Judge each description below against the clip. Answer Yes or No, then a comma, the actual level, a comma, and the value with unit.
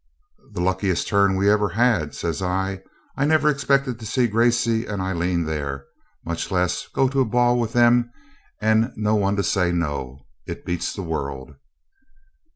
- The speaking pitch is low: Yes, low, 100 Hz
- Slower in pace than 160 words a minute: No, average, 170 wpm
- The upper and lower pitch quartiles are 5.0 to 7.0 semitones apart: Yes, average, 5.3 semitones